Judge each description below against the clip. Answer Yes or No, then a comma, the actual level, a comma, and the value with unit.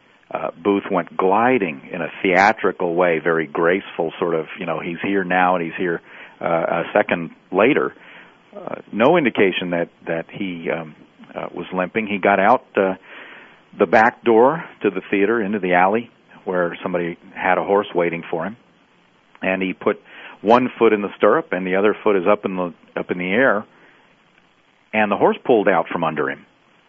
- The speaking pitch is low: Yes, very low, 95 Hz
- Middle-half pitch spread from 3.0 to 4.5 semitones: No, narrow, 2.5 semitones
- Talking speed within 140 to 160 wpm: No, average, 185 wpm